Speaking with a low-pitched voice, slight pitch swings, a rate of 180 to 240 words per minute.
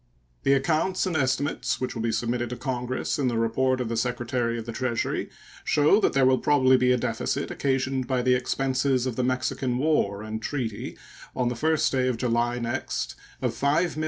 Yes: low, 130 Hz; narrow, 2.0 semitones; average, 195 wpm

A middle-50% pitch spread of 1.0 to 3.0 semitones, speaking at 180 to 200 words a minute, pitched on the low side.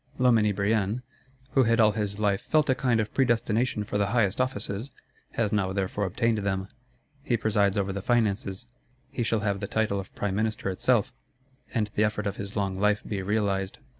Yes: narrow, 2.5 semitones; average, 190 wpm; low, 105 Hz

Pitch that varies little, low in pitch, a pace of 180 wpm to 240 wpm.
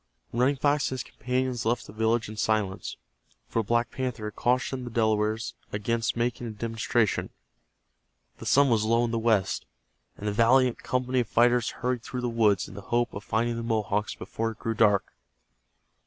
Yes: narrow, 2.1 semitones; low, 115 Hz; average, 185 wpm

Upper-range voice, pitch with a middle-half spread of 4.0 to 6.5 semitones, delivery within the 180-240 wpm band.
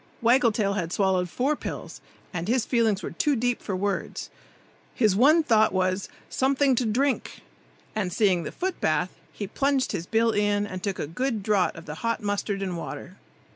Yes: high, 210 Hz; average, 4.8 semitones; average, 185 wpm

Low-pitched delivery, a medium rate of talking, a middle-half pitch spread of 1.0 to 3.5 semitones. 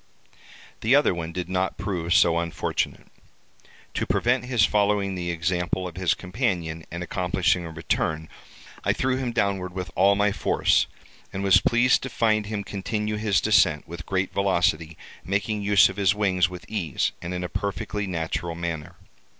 Yes: very low, 95 Hz; average, 165 wpm; average, 3.2 semitones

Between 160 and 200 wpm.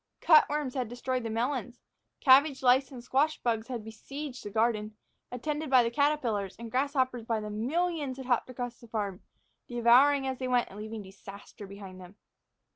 Yes: average, 170 wpm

